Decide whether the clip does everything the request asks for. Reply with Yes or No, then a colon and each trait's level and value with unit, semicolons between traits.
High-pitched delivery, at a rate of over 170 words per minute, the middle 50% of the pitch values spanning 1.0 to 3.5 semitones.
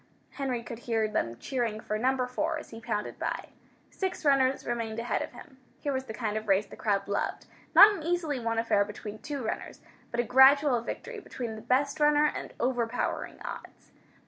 No: high, 245 Hz; average, 195 wpm; average, 4.2 semitones